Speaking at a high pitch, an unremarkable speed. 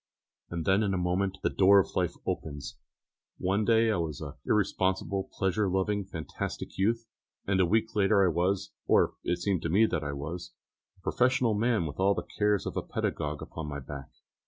No: very low, 95 Hz; average, 195 wpm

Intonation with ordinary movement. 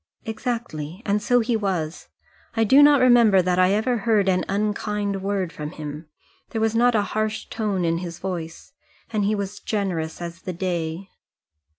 Yes: average, 3.8 semitones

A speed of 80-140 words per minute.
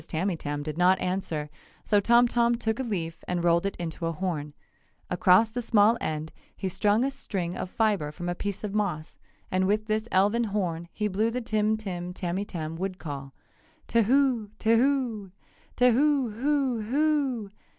No: average, 160 wpm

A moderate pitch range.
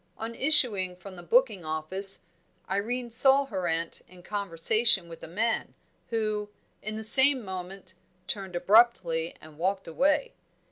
Yes: average, 4.6 semitones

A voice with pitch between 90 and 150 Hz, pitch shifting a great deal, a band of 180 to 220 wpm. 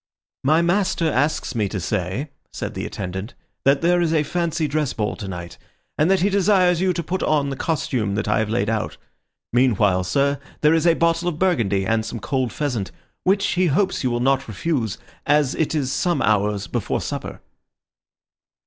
Yes: medium, 140 Hz; wide, 7.5 semitones; average, 185 wpm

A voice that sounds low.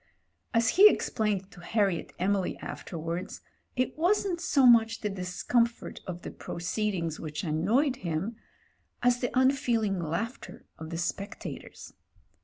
No: high, 210 Hz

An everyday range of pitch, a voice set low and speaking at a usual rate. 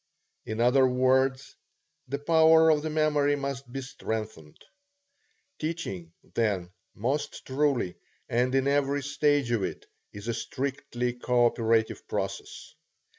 No: average, 3.5 semitones; low, 130 Hz; slow, 125 wpm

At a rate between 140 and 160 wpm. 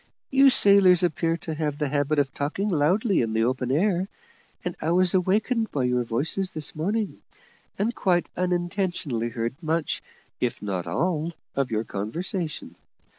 Yes: average, 155 wpm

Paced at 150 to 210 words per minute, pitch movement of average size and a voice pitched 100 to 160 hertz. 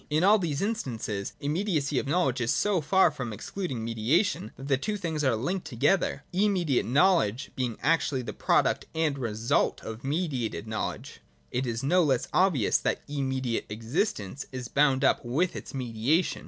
No: average, 175 wpm; wide, 6.4 semitones; medium, 140 Hz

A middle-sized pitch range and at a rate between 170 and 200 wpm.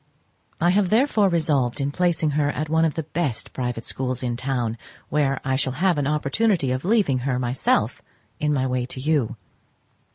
Yes: average, 4.2 semitones; average, 185 wpm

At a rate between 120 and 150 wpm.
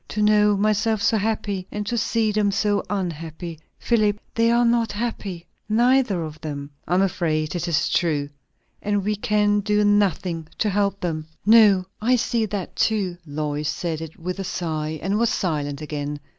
No: average, 180 wpm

